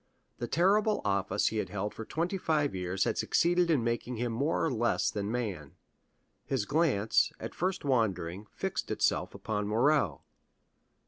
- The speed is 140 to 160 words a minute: Yes, average, 155 wpm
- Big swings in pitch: Yes, wide, 7.1 semitones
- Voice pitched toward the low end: Yes, low, 115 Hz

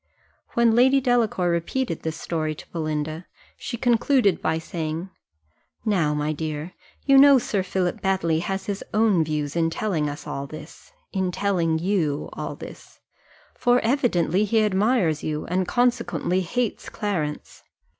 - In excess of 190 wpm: No, average, 145 wpm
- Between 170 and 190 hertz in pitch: Yes, medium, 185 Hz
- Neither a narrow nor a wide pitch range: No, wide, 5.9 semitones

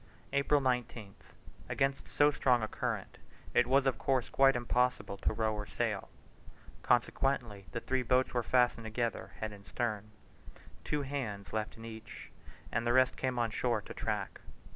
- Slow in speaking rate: No, average, 165 wpm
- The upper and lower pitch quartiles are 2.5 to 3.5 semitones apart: Yes, average, 3.1 semitones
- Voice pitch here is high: No, low, 120 Hz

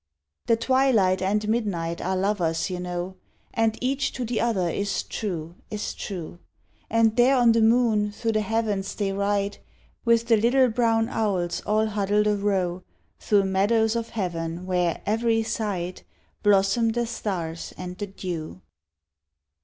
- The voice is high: Yes, high, 205 Hz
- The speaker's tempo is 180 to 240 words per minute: No, average, 145 wpm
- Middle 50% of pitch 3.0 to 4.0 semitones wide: Yes, average, 3.6 semitones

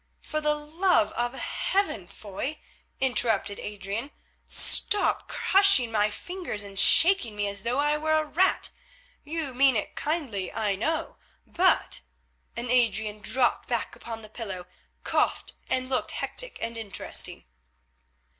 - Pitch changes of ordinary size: No, wide, 6.8 semitones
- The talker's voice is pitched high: Yes, high, 245 Hz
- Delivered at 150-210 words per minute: No, slow, 135 wpm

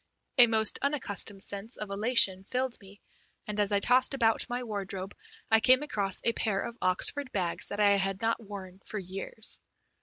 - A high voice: Yes, high, 210 Hz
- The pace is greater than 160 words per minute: Yes, average, 180 wpm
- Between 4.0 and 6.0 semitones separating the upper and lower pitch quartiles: No, average, 3.2 semitones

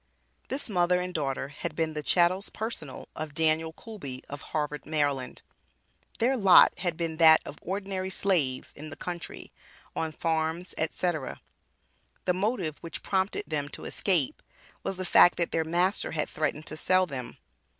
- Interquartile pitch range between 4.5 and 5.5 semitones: No, average, 3.3 semitones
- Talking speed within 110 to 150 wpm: No, average, 160 wpm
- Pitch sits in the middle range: Yes, medium, 165 Hz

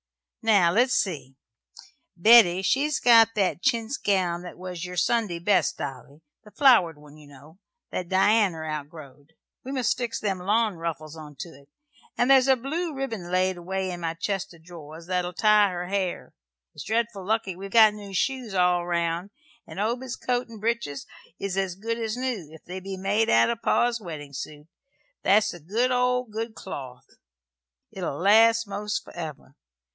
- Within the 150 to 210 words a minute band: Yes, average, 170 wpm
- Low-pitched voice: No, high, 190 Hz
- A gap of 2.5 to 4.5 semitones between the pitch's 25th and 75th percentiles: No, average, 5.1 semitones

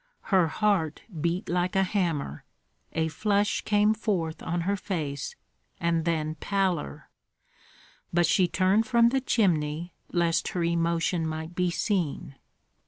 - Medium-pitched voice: Yes, medium, 175 Hz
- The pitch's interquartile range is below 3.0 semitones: No, average, 3.7 semitones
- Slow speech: Yes, slow, 130 wpm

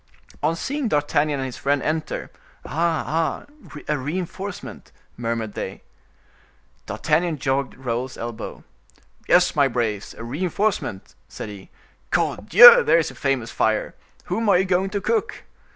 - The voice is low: No, medium, 150 Hz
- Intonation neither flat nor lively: No, wide, 7.0 semitones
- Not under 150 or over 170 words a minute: No, slow, 135 wpm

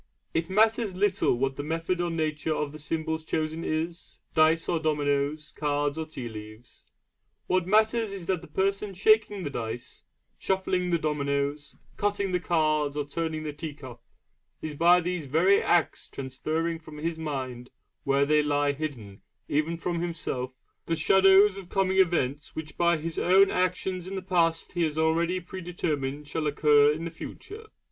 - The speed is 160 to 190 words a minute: Yes, average, 170 wpm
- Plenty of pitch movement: No, average, 3.7 semitones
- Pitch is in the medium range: Yes, medium, 160 Hz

